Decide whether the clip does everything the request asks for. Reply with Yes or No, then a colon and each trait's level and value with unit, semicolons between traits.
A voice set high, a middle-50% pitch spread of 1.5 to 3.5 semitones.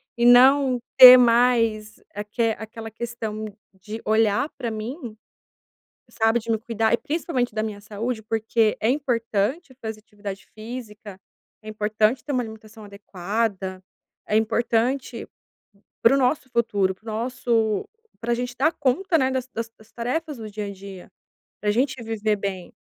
Yes: high, 225 Hz; narrow, 2.6 semitones